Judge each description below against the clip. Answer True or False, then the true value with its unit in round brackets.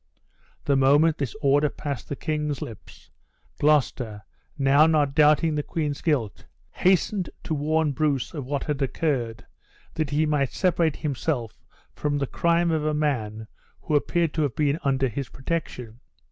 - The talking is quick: False (155 wpm)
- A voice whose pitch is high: False (145 Hz)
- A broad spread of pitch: False (2.4 semitones)